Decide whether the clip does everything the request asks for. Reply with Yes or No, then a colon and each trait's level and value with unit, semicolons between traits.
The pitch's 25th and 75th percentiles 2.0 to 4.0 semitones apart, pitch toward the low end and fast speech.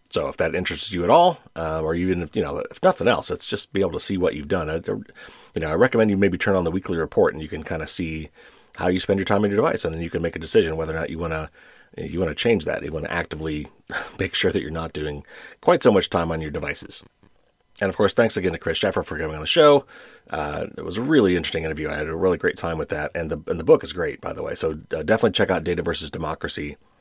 Yes: average, 3.5 semitones; very low, 85 Hz; fast, 295 wpm